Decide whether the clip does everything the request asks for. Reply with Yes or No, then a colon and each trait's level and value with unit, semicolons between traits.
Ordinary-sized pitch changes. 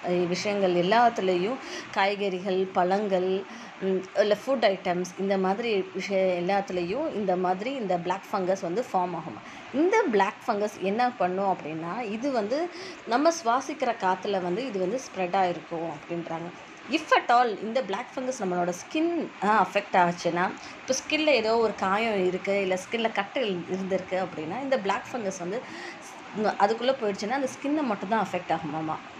Yes: average, 4.5 semitones